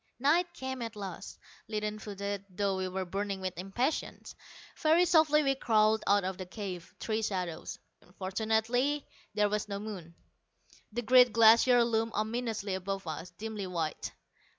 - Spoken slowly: No, average, 150 wpm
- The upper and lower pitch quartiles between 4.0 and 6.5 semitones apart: No, average, 3.6 semitones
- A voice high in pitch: Yes, high, 210 Hz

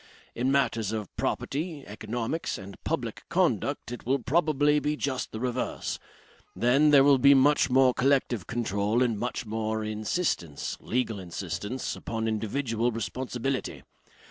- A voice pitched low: Yes, low, 120 Hz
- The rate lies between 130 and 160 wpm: Yes, slow, 135 wpm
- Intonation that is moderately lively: Yes, average, 4.0 semitones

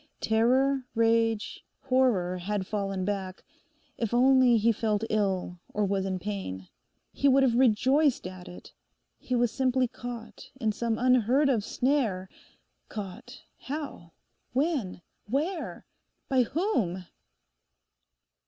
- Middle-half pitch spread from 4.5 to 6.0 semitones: Yes, average, 4.9 semitones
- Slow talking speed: Yes, slow, 115 wpm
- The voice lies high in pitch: Yes, high, 230 Hz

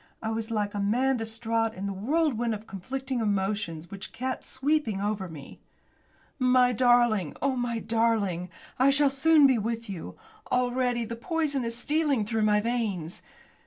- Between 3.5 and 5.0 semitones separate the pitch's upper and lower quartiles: Yes, average, 3.8 semitones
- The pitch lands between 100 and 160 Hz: No, high, 230 Hz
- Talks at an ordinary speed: Yes, average, 160 wpm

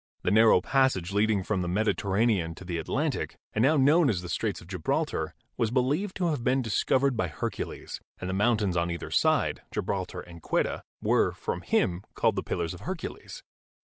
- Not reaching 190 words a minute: No, average, 195 wpm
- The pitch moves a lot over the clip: Yes, wide, 6.5 semitones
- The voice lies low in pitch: Yes, low, 105 Hz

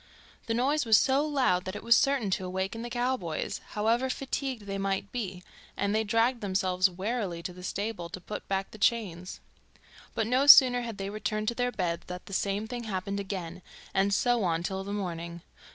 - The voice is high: Yes, high, 205 Hz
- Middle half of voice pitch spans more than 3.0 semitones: Yes, average, 4.1 semitones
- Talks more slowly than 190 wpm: No, average, 200 wpm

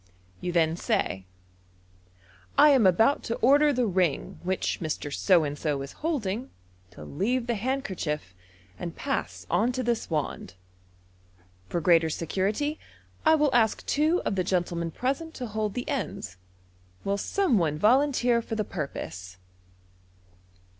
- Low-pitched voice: No, high, 200 Hz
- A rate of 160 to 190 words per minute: No, average, 145 wpm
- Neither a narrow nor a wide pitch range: No, wide, 7.9 semitones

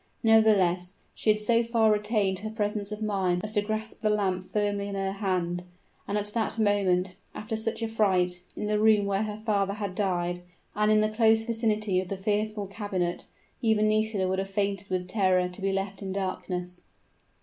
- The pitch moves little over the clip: Yes, narrow, 2.3 semitones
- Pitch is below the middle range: No, high, 205 Hz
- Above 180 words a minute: Yes, average, 195 wpm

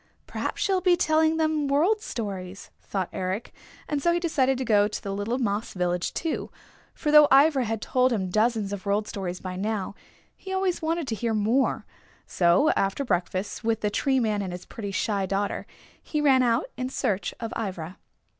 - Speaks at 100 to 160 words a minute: No, average, 190 wpm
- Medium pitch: No, high, 225 Hz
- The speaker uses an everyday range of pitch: No, wide, 6.3 semitones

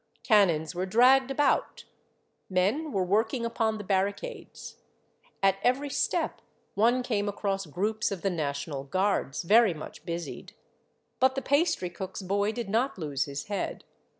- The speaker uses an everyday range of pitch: Yes, average, 4.8 semitones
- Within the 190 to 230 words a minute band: No, average, 145 wpm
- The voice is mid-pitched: No, high, 200 Hz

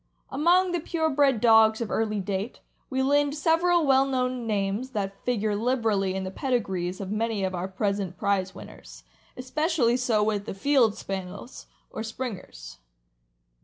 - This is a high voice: Yes, high, 225 Hz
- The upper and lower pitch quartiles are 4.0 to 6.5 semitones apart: Yes, average, 5.1 semitones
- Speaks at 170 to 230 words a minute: No, average, 155 wpm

